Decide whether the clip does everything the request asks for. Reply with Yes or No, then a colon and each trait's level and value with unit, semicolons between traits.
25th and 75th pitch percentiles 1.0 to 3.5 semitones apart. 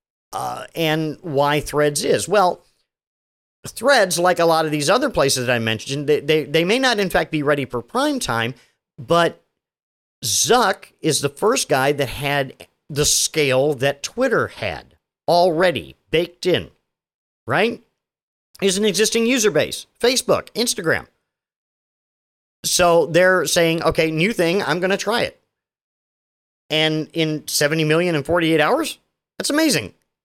No: average, 4.4 semitones